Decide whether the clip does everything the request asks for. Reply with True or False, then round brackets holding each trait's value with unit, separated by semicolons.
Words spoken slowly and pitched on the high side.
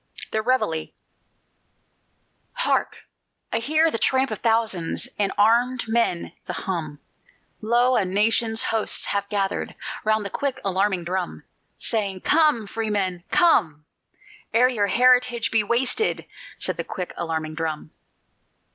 True (130 wpm; 215 Hz)